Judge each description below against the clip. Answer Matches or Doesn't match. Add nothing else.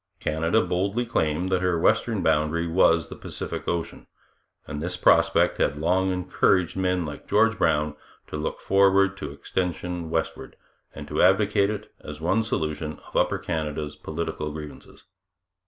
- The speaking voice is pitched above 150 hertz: Doesn't match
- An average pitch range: Matches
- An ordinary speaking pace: Matches